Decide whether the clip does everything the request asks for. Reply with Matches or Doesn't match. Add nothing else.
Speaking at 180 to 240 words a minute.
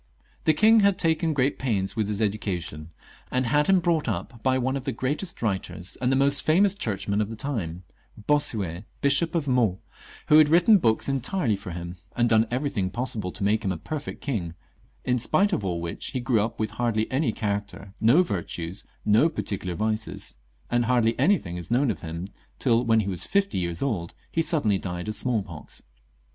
Matches